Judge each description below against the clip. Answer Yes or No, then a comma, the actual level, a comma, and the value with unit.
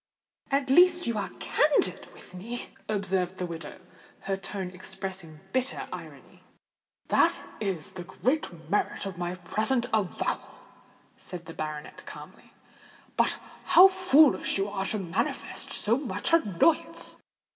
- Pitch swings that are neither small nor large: No, wide, 6.4 semitones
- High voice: Yes, high, 195 Hz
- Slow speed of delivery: Yes, slow, 130 wpm